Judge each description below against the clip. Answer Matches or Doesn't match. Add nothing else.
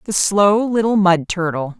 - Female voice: Matches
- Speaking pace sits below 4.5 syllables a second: Matches